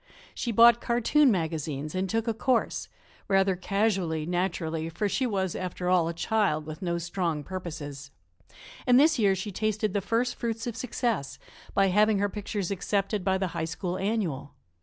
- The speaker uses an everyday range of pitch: Yes, average, 4.4 semitones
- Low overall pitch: No, high, 195 Hz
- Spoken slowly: No, average, 170 wpm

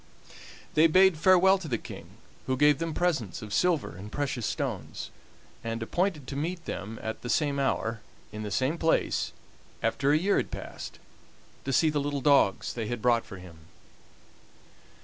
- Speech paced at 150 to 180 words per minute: Yes, average, 170 wpm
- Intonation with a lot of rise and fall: Yes, wide, 6.3 semitones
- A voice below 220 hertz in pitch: Yes, medium, 140 Hz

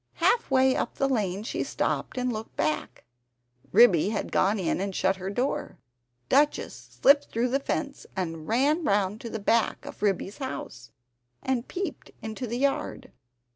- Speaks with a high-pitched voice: Yes, high, 225 Hz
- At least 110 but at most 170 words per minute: Yes, average, 165 wpm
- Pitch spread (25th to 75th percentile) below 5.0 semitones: No, average, 5.3 semitones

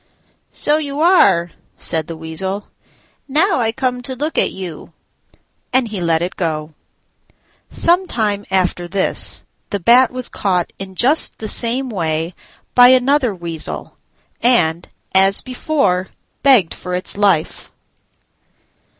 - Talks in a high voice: Yes, high, 200 Hz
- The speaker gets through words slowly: Yes, slow, 130 wpm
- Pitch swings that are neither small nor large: No, wide, 6.6 semitones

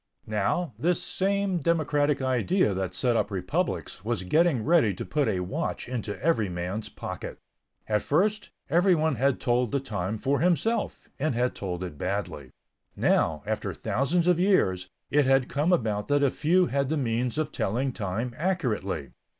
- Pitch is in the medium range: No, low, 130 Hz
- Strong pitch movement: Yes, wide, 7.5 semitones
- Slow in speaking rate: No, average, 165 wpm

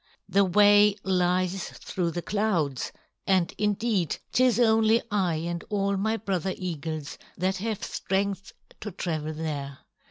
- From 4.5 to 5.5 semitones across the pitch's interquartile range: No, average, 3.4 semitones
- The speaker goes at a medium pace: No, slow, 130 wpm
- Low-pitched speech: No, high, 190 Hz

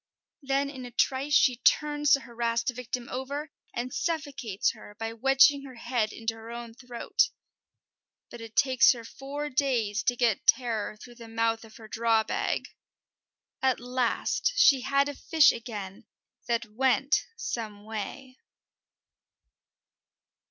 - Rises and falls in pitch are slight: No, average, 3.2 semitones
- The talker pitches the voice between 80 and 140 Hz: No, high, 245 Hz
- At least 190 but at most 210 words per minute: No, average, 140 wpm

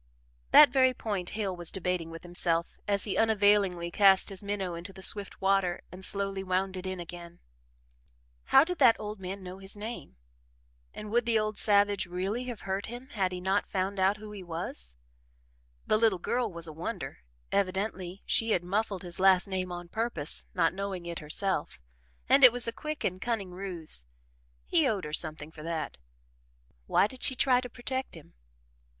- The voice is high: Yes, high, 195 Hz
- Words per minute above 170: Yes, average, 185 wpm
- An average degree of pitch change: Yes, average, 3.3 semitones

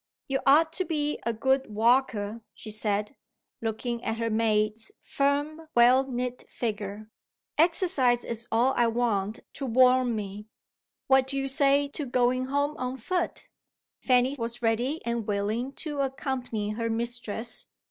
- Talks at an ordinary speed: Yes, average, 145 wpm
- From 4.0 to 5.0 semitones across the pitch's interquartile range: No, average, 3.3 semitones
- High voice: Yes, high, 245 Hz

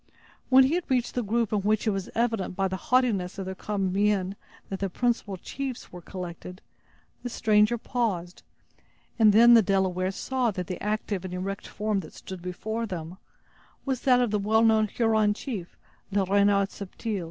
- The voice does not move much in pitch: No, average, 3.4 semitones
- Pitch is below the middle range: No, high, 205 Hz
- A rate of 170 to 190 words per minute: Yes, average, 185 wpm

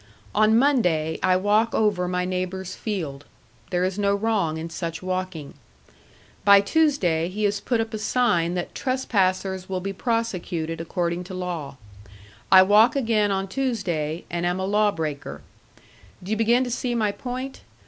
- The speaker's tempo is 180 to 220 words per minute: No, average, 160 wpm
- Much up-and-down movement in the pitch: No, average, 3.9 semitones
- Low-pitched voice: No, high, 190 Hz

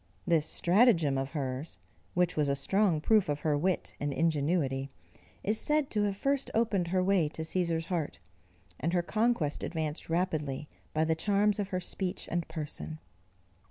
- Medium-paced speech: Yes, average, 165 wpm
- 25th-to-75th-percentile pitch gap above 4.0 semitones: Yes, average, 4.6 semitones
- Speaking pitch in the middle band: Yes, medium, 170 Hz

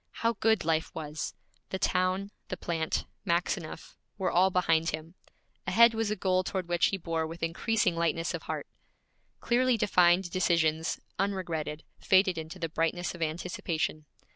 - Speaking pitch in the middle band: Yes, medium, 175 Hz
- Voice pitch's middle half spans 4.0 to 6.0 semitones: No, average, 2.7 semitones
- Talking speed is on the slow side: No, average, 150 wpm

